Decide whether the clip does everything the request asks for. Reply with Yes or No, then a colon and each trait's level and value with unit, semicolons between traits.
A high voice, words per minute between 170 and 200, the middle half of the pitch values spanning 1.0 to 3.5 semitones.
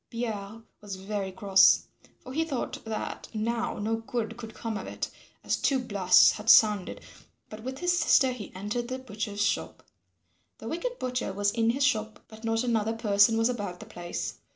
Yes: high, 225 Hz; average, 180 wpm; average, 3.0 semitones